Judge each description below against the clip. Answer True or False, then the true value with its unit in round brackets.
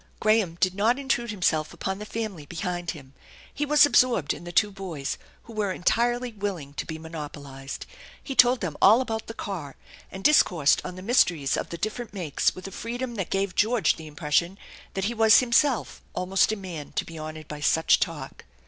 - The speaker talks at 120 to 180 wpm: False (195 wpm)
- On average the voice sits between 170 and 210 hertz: True (190 Hz)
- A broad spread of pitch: True (5.9 semitones)